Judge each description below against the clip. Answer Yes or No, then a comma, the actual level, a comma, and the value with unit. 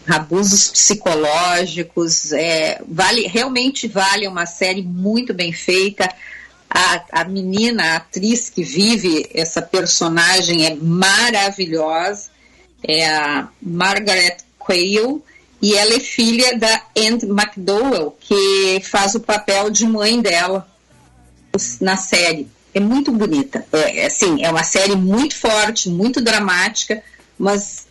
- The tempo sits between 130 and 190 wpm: No, slow, 120 wpm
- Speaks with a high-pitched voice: Yes, high, 195 Hz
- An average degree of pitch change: Yes, average, 4.0 semitones